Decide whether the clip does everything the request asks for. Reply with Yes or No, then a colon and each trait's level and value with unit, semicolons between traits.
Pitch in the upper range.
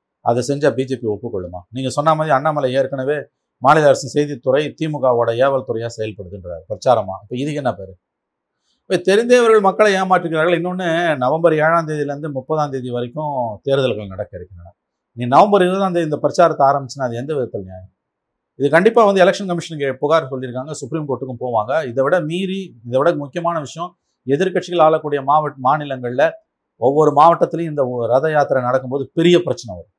No: medium, 145 Hz